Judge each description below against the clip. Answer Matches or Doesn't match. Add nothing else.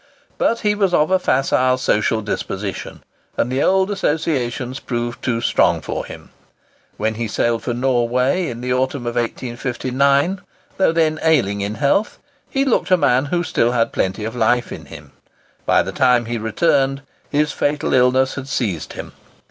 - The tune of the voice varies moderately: Matches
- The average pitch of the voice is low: Matches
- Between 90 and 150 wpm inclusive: Doesn't match